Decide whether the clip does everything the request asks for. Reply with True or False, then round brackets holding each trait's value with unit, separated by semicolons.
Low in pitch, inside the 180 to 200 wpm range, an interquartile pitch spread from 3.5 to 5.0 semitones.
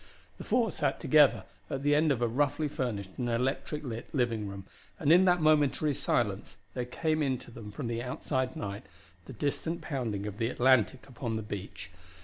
True (130 Hz; 190 wpm; 4.4 semitones)